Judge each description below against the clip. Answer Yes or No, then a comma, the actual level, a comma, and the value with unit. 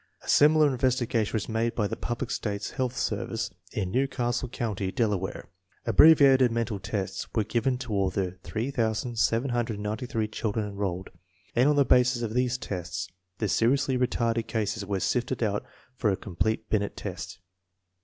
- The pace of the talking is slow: No, average, 165 wpm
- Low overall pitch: Yes, low, 115 Hz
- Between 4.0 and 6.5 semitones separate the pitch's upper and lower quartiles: No, average, 3.5 semitones